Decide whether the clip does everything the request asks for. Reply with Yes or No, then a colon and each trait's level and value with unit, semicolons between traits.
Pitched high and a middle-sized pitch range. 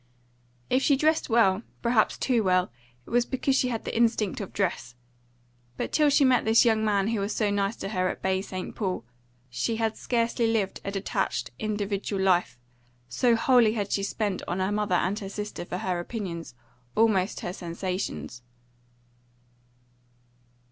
Yes: high, 205 Hz; average, 3.5 semitones